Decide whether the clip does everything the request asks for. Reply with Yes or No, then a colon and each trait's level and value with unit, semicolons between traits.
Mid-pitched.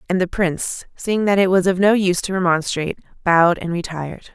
Yes: medium, 180 Hz